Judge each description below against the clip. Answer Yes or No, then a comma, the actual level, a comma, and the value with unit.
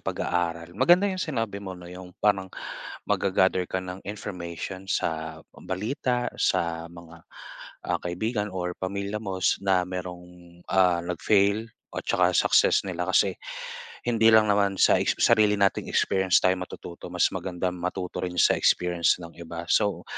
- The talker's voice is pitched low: Yes, very low, 95 Hz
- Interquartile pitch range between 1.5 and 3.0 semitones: Yes, narrow, 2.6 semitones